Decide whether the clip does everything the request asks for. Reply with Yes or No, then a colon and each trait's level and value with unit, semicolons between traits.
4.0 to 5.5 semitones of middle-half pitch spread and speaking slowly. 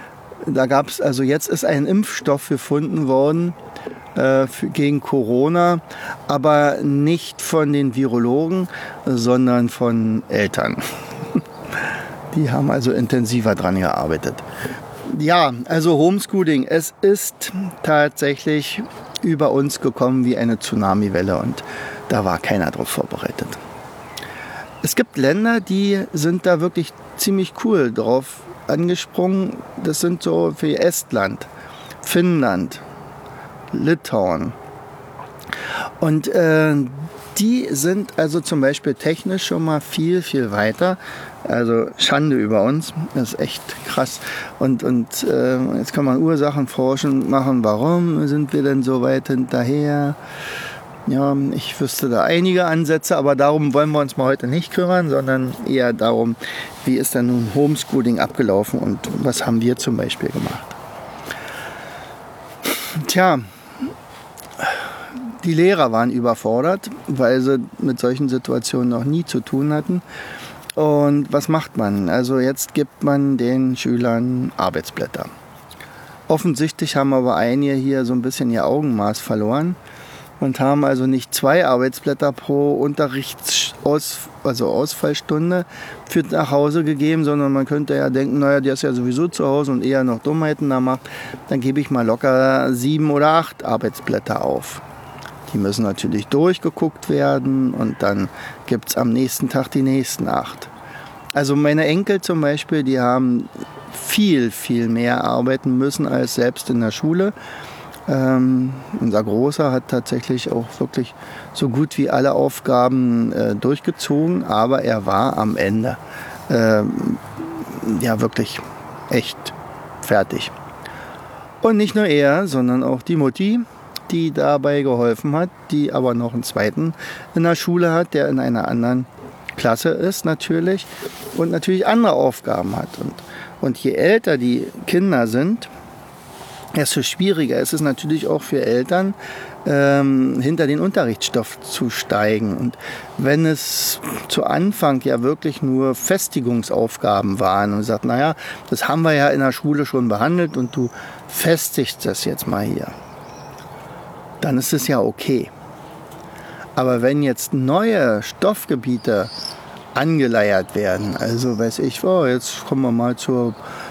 No: average, 4.4 semitones; average, 135 wpm